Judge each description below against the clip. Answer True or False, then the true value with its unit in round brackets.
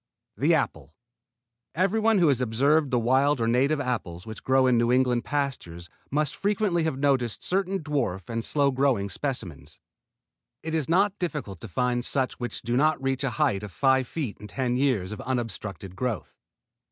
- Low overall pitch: True (130 Hz)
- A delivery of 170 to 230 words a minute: True (175 wpm)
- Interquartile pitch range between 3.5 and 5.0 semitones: True (4.2 semitones)